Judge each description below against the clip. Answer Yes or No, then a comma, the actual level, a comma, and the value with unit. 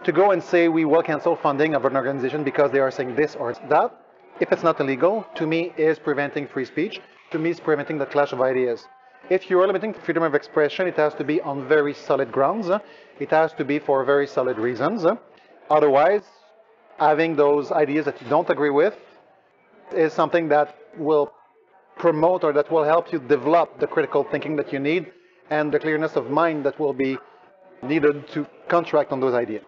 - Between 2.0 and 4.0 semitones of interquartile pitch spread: Yes, average, 2.8 semitones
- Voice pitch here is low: No, medium, 150 Hz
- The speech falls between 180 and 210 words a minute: Yes, average, 200 wpm